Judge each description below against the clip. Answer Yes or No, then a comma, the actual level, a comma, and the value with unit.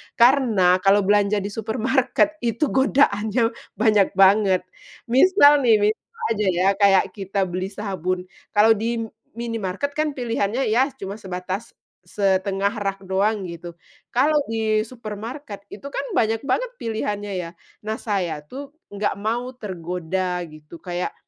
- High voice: Yes, high, 210 Hz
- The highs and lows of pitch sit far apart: No, average, 3.7 semitones